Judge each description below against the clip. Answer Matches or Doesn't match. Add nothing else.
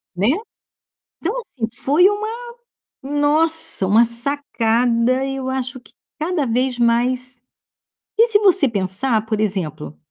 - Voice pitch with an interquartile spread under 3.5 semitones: Doesn't match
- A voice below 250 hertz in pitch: Doesn't match